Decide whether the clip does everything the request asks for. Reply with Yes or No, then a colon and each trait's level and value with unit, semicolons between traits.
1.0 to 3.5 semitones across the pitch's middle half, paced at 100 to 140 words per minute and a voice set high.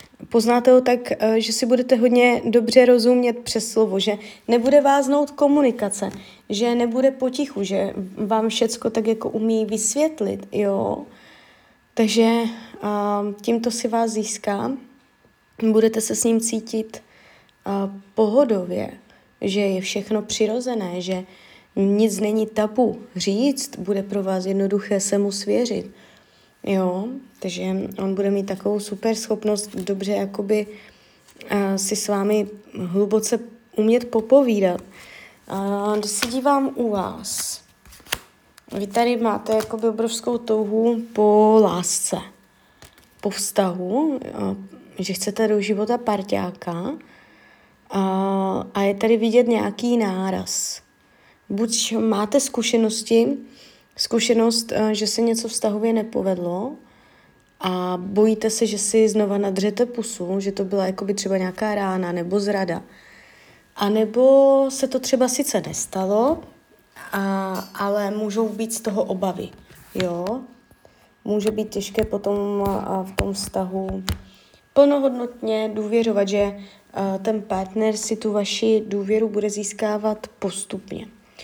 Yes: narrow, 2.6 semitones; average, 120 wpm; high, 215 Hz